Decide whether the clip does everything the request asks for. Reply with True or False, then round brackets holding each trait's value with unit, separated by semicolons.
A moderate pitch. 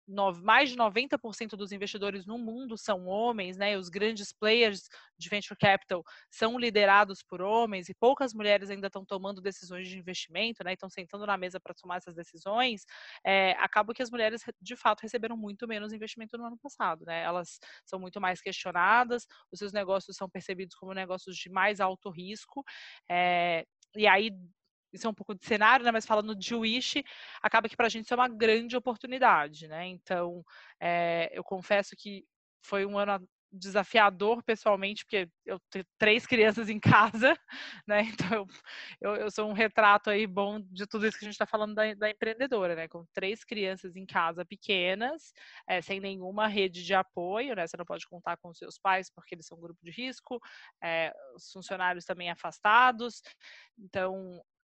False (200 Hz)